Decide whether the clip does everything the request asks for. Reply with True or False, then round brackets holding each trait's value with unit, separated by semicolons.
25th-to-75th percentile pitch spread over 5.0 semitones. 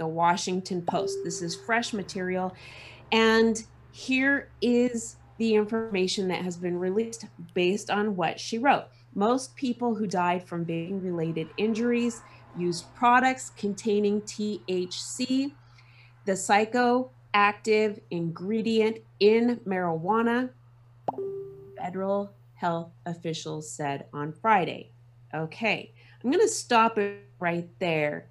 True (5.4 semitones)